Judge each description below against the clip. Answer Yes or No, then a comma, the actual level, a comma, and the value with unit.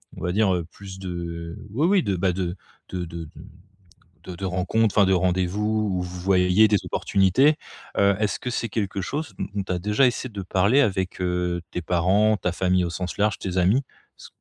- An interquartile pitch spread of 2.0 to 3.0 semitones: Yes, average, 2.7 semitones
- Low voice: Yes, very low, 95 Hz